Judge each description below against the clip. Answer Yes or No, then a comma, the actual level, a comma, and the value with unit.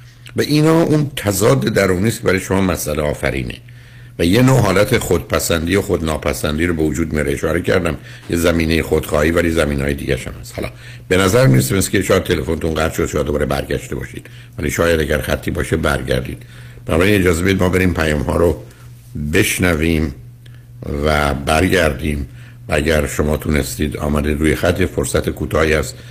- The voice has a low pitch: Yes, very low, 85 Hz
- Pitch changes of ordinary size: No, wide, 7.7 semitones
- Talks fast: Yes, fast, 165 wpm